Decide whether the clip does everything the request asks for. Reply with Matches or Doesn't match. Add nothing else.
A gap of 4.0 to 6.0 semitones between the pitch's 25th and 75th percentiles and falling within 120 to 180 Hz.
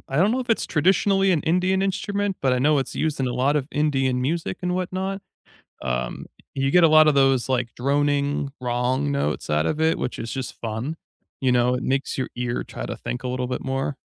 Matches